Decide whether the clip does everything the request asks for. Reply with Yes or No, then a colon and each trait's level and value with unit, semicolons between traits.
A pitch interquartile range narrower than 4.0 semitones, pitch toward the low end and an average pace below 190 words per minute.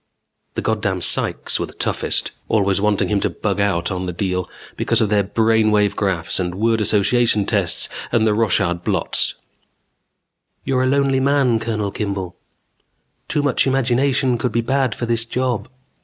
Yes: average, 3.6 semitones; low, 110 Hz; average, 165 wpm